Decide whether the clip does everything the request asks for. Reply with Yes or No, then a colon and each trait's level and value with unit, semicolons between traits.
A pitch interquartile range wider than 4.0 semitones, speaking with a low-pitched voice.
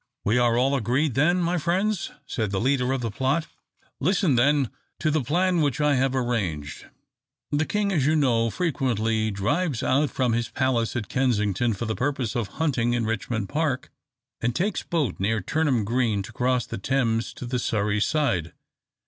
Yes: average, 4.7 semitones; low, 125 Hz